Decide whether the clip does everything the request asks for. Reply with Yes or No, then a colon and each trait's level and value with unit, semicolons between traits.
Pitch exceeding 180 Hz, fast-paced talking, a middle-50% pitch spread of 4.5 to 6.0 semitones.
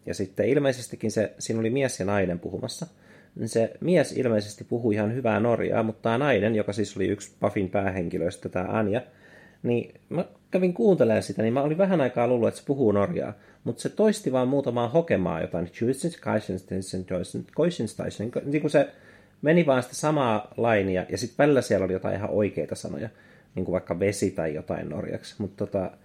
No: low, 110 Hz; fast, 175 wpm; average, 5.1 semitones